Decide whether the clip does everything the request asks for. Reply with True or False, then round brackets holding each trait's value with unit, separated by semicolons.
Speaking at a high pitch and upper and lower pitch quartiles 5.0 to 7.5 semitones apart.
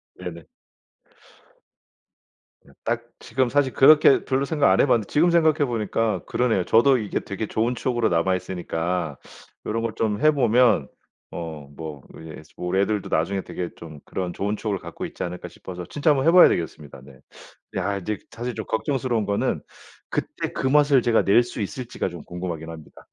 False (110 Hz; 6.1 semitones)